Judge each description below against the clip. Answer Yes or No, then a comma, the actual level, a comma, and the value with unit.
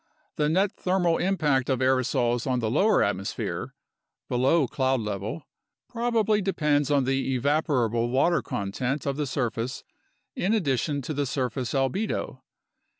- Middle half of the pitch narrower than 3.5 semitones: No, average, 4.5 semitones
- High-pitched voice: No, low, 135 Hz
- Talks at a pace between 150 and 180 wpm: No, average, 140 wpm